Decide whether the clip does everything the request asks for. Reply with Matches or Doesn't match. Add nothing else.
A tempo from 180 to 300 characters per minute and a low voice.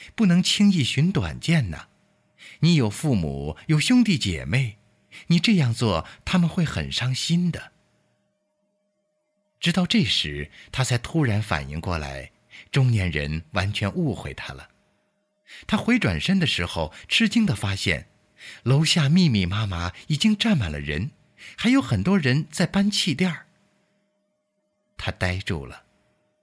Doesn't match